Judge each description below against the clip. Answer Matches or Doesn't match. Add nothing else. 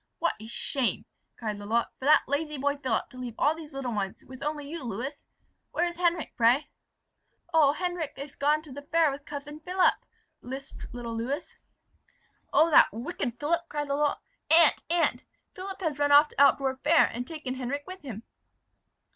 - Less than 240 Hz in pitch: Doesn't match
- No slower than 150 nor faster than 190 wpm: Matches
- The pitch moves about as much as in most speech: Matches